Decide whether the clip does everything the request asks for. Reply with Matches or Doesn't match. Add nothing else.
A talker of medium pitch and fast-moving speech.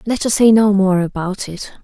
Doesn't match